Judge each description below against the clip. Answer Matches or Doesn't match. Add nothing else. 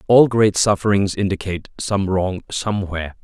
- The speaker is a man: Matches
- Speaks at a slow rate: Matches